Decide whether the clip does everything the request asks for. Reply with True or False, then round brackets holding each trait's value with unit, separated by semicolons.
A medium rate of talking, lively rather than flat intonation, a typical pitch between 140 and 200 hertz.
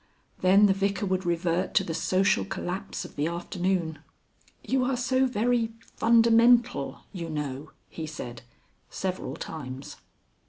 False (130 wpm; 5.8 semitones; 185 Hz)